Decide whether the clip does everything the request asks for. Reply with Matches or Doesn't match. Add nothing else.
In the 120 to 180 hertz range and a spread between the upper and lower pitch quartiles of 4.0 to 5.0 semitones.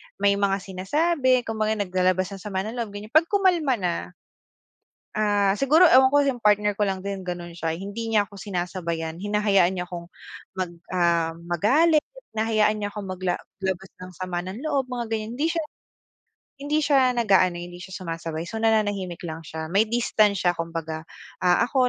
Doesn't match